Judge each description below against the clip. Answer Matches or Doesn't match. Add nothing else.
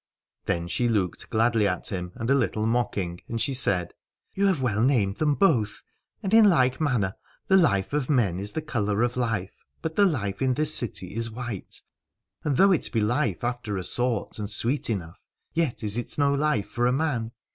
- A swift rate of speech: Matches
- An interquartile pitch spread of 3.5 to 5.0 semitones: Doesn't match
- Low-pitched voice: Matches